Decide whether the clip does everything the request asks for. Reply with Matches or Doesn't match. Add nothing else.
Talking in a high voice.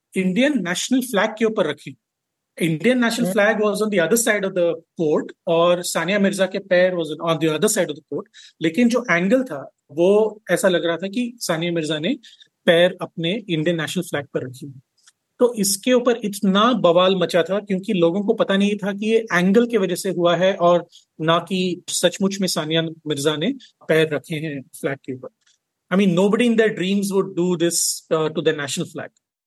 Doesn't match